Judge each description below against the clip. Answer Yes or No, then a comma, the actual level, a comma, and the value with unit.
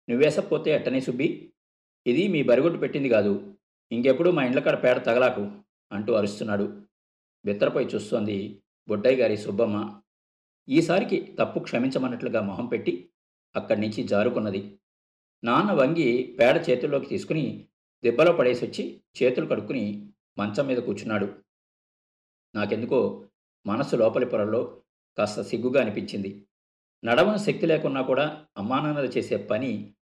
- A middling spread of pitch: Yes, average, 4.4 semitones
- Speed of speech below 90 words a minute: No, average, 110 wpm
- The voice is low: Yes, low, 105 Hz